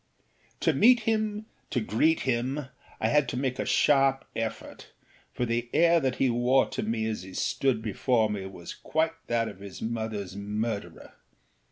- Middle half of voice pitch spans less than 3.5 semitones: No, average, 3.8 semitones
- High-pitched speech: No, low, 120 Hz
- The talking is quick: No, average, 170 wpm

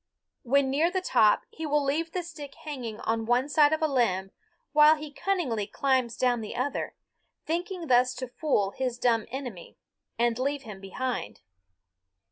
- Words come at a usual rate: Yes, average, 165 wpm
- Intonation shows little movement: No, average, 4.4 semitones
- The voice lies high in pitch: Yes, very high, 260 Hz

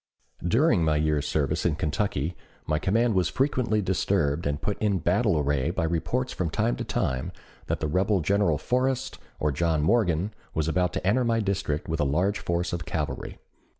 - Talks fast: No, average, 185 wpm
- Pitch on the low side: Yes, very low, 85 Hz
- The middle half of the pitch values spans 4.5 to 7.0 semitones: Yes, average, 5.0 semitones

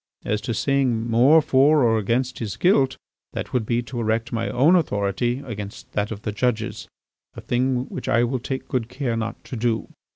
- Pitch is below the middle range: Yes, low, 120 Hz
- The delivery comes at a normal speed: Yes, average, 195 wpm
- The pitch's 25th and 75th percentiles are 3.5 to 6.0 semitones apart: No, average, 2.8 semitones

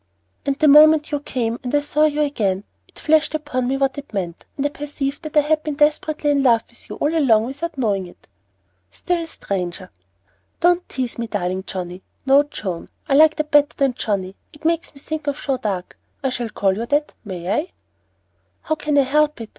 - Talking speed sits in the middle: No, fast, 210 wpm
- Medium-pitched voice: No, very high, 280 Hz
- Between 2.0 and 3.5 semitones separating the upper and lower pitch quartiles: No, average, 5.2 semitones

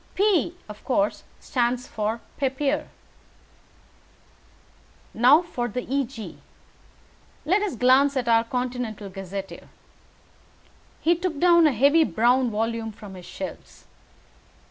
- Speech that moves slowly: Yes, slow, 110 wpm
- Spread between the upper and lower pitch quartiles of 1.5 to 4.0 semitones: No, average, 4.6 semitones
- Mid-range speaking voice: No, very high, 250 Hz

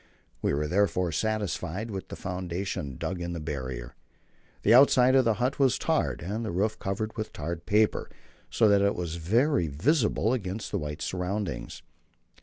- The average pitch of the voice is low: Yes, very low, 95 Hz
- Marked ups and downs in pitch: No, average, 4.5 semitones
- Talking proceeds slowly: No, average, 170 wpm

